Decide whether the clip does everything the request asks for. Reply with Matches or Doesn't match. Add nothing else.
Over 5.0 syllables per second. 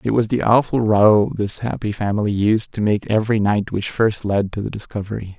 Matches